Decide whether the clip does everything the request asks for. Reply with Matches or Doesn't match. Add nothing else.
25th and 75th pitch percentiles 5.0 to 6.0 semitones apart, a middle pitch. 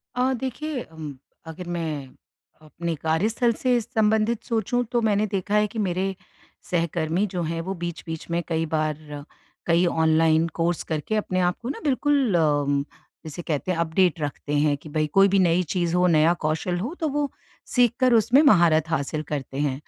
Matches